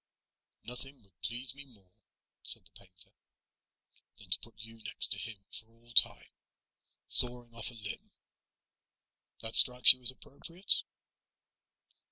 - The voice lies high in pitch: No, low, 115 Hz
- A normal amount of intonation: No, narrow, 2.2 semitones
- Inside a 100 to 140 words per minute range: Yes, slow, 135 wpm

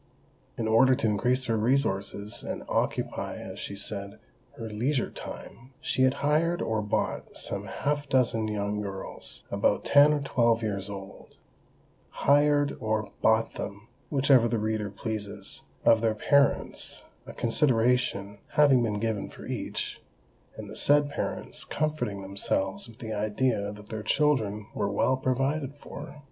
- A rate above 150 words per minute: No, average, 145 wpm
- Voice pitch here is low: Yes, low, 115 Hz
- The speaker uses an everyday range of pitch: Yes, average, 4.7 semitones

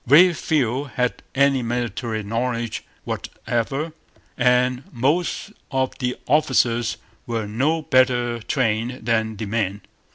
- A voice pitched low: Yes, low, 125 Hz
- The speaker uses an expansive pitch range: No, average, 2.7 semitones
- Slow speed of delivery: Yes, slow, 110 wpm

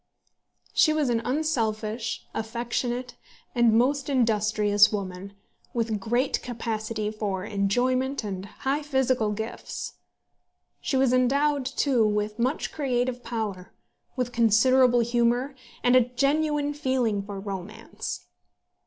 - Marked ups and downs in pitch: No, average, 3.4 semitones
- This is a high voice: Yes, high, 240 Hz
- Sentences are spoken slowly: Yes, slow, 110 wpm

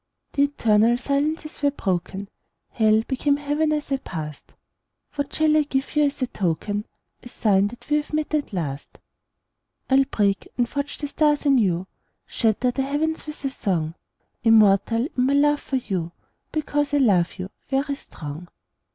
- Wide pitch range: Yes, wide, 6.3 semitones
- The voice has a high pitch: Yes, very high, 265 Hz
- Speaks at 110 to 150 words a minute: No, average, 165 wpm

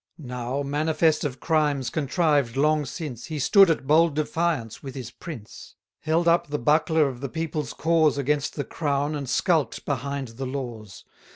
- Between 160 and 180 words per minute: Yes, average, 165 wpm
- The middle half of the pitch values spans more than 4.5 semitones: No, average, 3.1 semitones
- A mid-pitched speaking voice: Yes, medium, 145 Hz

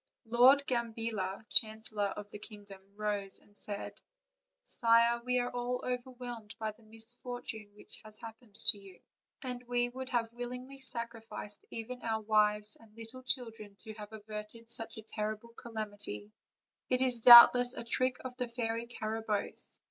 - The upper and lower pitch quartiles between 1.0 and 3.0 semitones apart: Yes, narrow, 2.5 semitones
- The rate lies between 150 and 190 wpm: Yes, average, 160 wpm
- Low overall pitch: No, high, 225 Hz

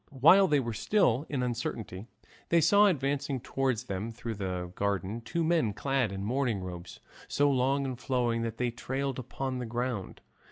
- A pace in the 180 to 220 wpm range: No, average, 170 wpm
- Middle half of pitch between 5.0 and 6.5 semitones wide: No, average, 3.8 semitones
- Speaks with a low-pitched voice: Yes, low, 125 Hz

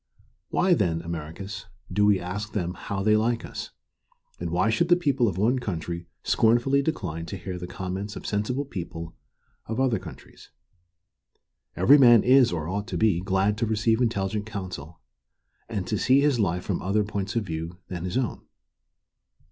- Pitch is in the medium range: No, low, 105 Hz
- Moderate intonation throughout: Yes, average, 4.5 semitones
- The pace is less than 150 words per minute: No, average, 170 wpm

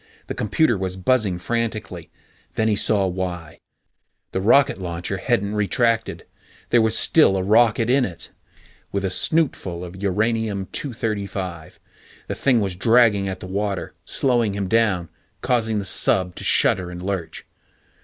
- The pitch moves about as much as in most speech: Yes, average, 3.7 semitones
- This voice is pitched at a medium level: No, low, 100 Hz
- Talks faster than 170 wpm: No, average, 145 wpm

